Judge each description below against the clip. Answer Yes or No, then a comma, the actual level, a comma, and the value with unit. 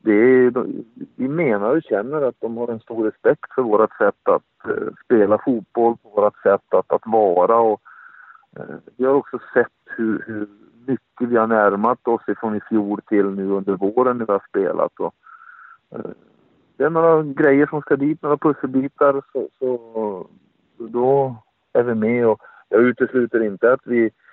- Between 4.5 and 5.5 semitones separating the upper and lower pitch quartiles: Yes, average, 4.8 semitones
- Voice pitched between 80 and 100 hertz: No, low, 125 Hz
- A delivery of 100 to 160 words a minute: No, average, 170 wpm